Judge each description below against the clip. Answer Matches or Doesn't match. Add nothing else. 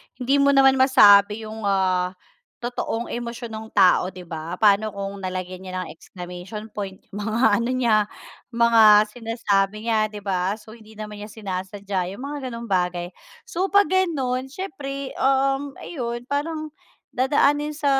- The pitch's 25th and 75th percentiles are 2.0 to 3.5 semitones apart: Doesn't match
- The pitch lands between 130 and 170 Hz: Doesn't match